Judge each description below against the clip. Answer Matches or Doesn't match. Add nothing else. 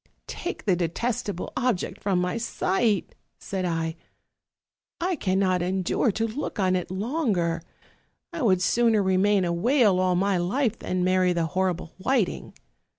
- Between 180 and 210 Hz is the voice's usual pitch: Matches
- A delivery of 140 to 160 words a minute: Matches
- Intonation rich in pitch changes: Doesn't match